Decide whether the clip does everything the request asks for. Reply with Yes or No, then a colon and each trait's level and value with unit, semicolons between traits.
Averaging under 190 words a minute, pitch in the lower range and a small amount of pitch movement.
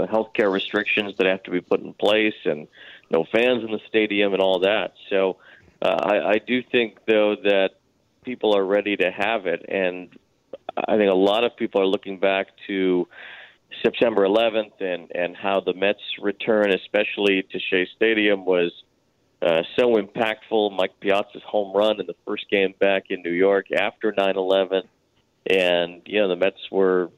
Yes: average, 175 wpm; low, 100 Hz; narrow, 2.0 semitones